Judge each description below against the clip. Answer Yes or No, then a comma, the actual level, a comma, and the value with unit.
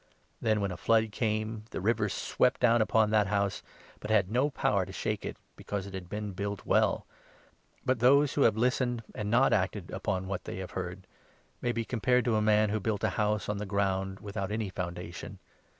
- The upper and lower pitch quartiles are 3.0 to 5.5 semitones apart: No, narrow, 2.4 semitones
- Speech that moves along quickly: Yes, fast, 210 wpm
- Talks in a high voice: No, low, 105 Hz